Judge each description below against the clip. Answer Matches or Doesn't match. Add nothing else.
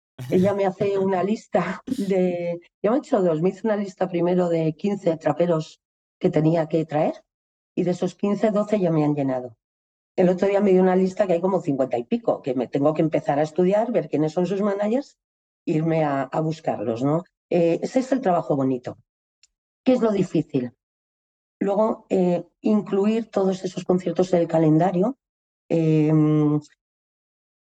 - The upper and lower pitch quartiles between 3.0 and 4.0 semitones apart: Doesn't match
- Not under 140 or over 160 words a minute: Doesn't match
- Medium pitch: Matches